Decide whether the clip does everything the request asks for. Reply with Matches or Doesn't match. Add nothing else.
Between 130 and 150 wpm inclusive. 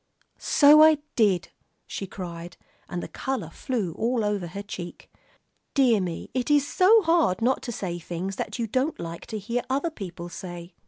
Doesn't match